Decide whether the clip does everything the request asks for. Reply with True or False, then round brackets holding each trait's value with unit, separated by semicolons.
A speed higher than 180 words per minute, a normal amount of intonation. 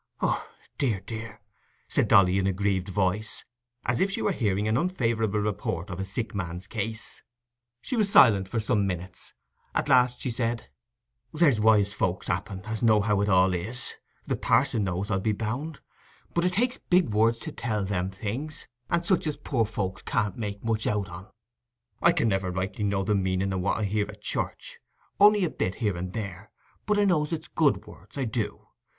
True (195 wpm; 4.4 semitones)